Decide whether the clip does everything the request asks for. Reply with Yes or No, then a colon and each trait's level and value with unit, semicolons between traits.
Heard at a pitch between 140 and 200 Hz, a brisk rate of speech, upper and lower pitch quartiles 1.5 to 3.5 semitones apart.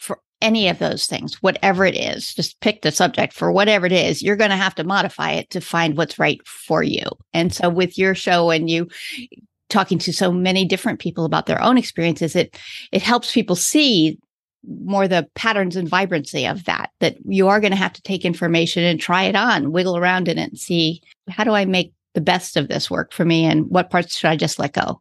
Yes: medium, 185 Hz; fast, 230 wpm; narrow, 2.5 semitones